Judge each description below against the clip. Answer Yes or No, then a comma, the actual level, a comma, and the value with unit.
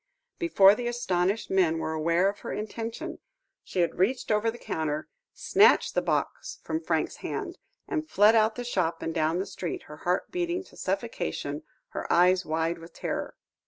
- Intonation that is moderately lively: No, wide, 6.1 semitones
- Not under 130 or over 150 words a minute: No, average, 180 wpm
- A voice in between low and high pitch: No, high, 195 Hz